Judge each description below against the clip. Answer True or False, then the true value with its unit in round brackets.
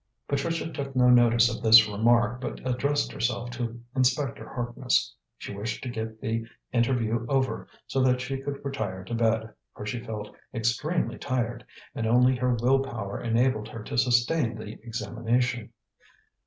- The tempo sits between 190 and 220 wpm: False (155 wpm)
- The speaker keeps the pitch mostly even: True (2.3 semitones)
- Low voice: True (120 Hz)